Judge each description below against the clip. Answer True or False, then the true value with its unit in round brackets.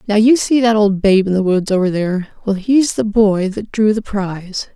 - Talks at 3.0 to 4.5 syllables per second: False (5.0 syllables/s)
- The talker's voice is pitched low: False (205 Hz)